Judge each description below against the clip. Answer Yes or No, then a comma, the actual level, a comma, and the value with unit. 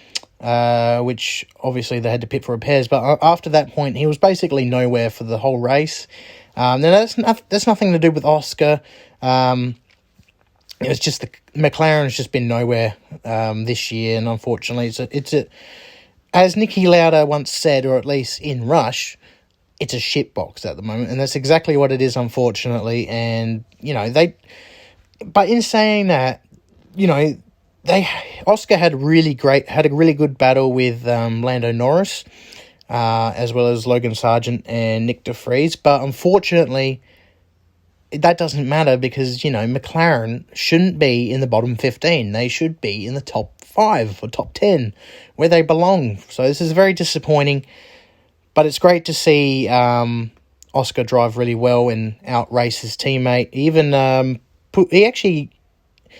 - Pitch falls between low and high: No, low, 130 Hz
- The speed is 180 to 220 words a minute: No, average, 165 wpm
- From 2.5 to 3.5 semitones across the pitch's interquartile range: No, average, 4.6 semitones